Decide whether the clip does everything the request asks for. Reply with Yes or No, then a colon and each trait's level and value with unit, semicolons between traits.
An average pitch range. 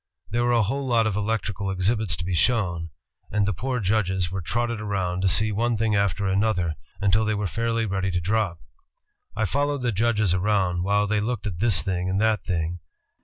Yes: average, 3.2 semitones